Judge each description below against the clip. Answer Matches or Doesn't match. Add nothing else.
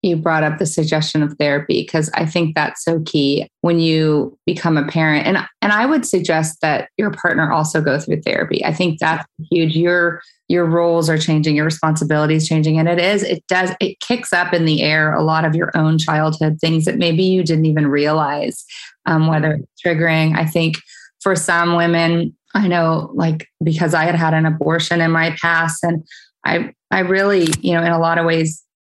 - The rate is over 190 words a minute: Matches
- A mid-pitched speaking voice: Matches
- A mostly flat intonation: Matches